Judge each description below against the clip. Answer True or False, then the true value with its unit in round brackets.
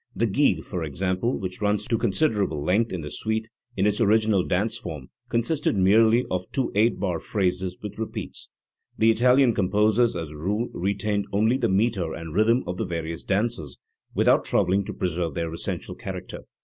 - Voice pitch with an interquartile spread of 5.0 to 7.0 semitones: False (3.9 semitones)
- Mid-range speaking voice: False (100 Hz)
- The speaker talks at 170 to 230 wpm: True (175 wpm)